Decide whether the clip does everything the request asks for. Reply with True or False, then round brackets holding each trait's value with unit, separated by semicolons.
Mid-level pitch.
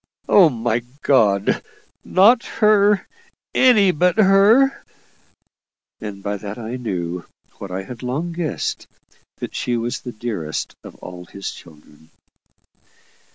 False (120 Hz)